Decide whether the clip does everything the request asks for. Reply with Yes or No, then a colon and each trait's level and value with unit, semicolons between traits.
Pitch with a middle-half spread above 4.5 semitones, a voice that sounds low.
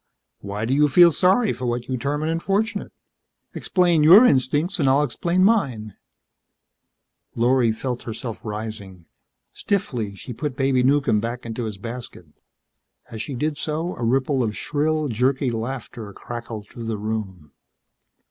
Yes: average, 5.1 semitones; low, 125 Hz